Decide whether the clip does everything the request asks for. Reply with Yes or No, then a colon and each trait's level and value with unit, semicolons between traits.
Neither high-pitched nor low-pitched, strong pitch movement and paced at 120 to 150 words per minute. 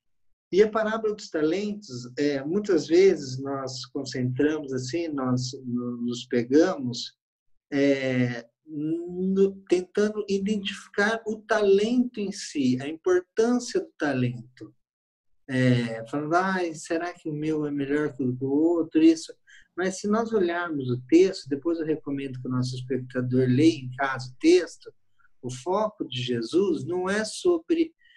Yes: medium, 160 Hz; wide, 8.3 semitones; average, 140 wpm